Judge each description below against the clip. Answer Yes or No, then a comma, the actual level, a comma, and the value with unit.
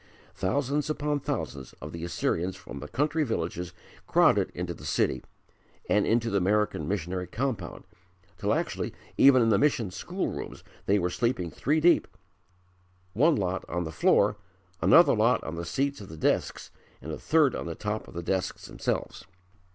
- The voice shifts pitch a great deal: Yes, wide, 7.8 semitones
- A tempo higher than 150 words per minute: Yes, average, 170 wpm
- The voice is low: Yes, low, 100 Hz